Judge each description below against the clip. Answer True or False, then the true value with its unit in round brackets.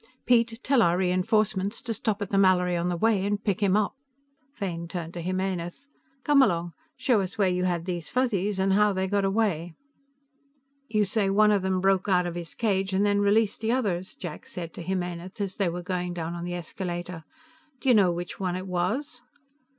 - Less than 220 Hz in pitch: True (190 Hz)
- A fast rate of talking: True (210 wpm)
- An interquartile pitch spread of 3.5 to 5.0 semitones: False (2.8 semitones)